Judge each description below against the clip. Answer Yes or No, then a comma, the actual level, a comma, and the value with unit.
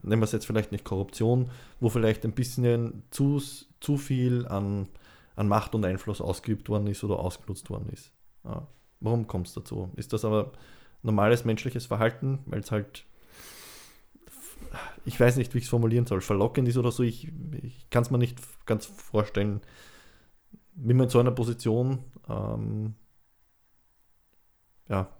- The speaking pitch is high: No, low, 110 Hz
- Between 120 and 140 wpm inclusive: No, average, 160 wpm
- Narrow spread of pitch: No, average, 3.4 semitones